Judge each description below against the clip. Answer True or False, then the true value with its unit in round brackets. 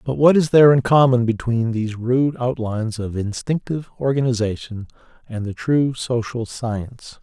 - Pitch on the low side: True (120 Hz)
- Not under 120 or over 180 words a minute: True (150 wpm)